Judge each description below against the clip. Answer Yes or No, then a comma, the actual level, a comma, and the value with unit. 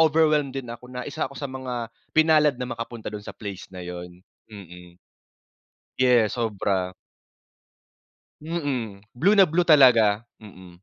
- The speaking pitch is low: Yes, low, 120 Hz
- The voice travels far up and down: Yes, wide, 6.0 semitones